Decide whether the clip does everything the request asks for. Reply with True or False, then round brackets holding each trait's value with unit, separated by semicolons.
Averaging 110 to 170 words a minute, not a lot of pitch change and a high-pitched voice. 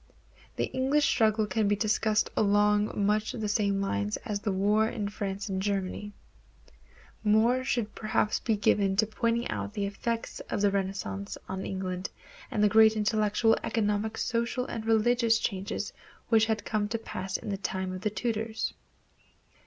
True (165 wpm; 1.9 semitones; 210 Hz)